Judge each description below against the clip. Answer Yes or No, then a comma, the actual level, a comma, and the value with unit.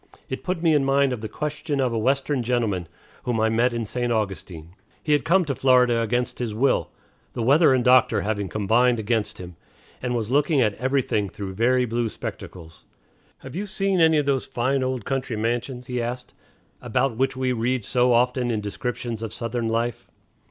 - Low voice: Yes, low, 125 Hz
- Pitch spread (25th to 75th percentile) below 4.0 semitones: Yes, average, 2.9 semitones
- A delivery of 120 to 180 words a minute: No, average, 195 wpm